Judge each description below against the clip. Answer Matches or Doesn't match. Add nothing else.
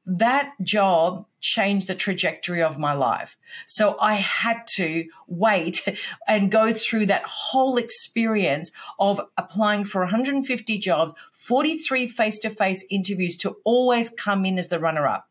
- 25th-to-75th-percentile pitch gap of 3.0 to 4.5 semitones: Matches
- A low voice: Doesn't match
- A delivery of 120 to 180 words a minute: Matches